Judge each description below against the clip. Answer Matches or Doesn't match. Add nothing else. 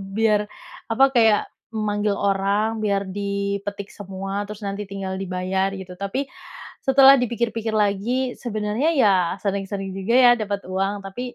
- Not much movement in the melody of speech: Matches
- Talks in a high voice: Matches